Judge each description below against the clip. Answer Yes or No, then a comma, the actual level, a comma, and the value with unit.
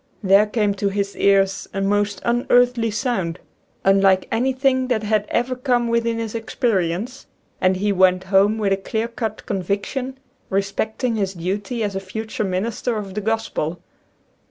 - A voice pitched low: No, high, 210 Hz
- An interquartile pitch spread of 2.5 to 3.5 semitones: Yes, average, 3.2 semitones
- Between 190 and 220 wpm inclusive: No, average, 155 wpm